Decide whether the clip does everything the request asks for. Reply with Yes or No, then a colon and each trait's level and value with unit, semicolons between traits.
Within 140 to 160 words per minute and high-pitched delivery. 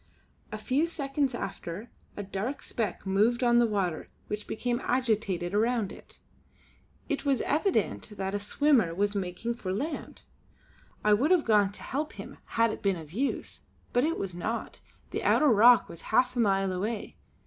No: average, 175 wpm; high, 220 Hz